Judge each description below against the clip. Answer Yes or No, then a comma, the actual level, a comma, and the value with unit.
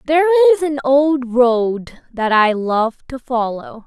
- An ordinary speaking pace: Yes, average, 155 wpm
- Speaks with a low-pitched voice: No, very high, 265 Hz